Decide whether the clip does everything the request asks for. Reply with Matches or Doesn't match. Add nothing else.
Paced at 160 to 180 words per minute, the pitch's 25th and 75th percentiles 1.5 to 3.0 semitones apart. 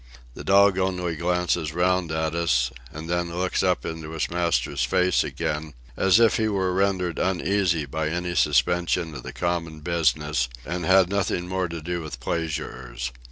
Matches